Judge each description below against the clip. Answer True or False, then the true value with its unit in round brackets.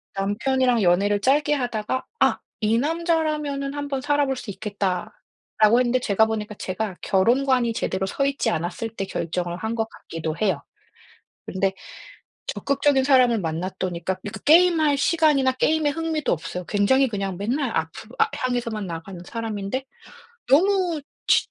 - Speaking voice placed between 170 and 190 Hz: False (230 Hz)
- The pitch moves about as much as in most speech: False (6.1 semitones)